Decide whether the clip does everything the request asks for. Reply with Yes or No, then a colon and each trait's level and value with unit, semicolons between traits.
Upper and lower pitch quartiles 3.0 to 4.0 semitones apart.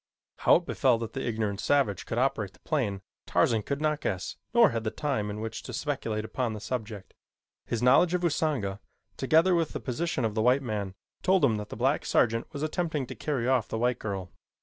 No: average, 5.3 semitones